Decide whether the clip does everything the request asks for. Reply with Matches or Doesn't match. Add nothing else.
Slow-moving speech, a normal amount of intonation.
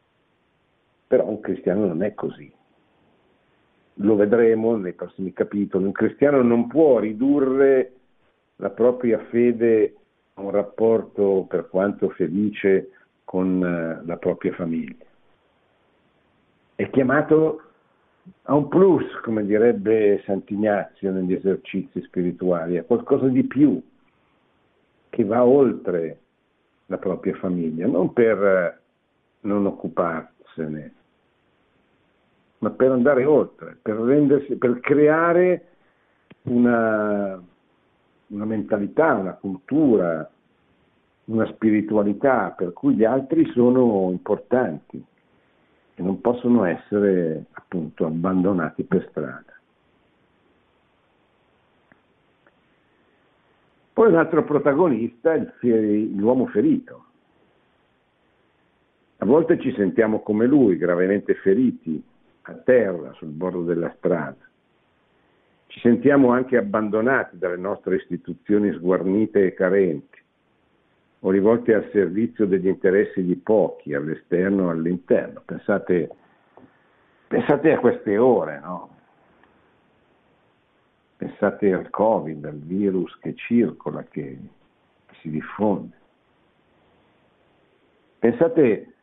Matches